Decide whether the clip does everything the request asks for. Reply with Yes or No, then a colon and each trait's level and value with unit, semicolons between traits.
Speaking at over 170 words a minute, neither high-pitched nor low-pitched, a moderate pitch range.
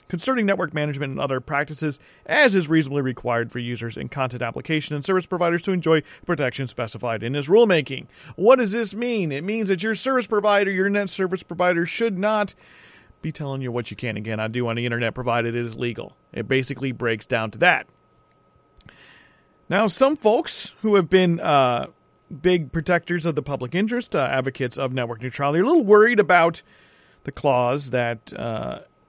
No: average, 185 wpm; medium, 155 Hz; wide, 7.6 semitones